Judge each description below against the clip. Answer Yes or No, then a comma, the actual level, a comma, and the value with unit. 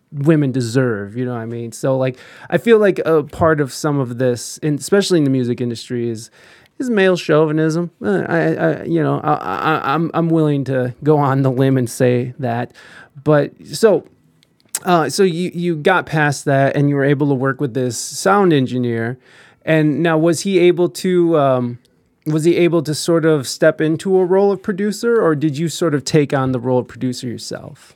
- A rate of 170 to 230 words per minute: Yes, average, 200 wpm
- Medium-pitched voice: Yes, medium, 150 Hz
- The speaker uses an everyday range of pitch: Yes, average, 4.7 semitones